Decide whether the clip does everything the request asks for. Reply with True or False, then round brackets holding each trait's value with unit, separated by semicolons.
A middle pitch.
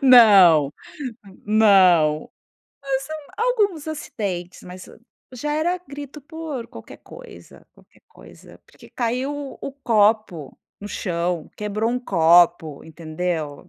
False (215 Hz)